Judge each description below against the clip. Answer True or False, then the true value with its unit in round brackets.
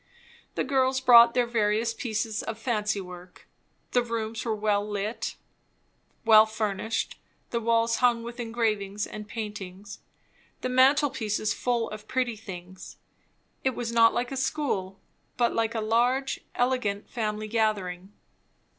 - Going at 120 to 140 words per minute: True (135 wpm)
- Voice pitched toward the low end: False (225 Hz)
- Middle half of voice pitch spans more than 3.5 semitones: False (2.4 semitones)